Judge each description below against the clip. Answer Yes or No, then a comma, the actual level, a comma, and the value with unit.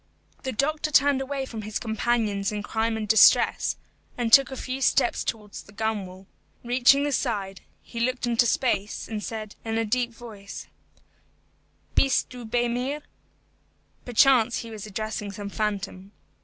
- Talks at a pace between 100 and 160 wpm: Yes, average, 155 wpm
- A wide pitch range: No, average, 3.2 semitones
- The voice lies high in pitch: Yes, high, 225 Hz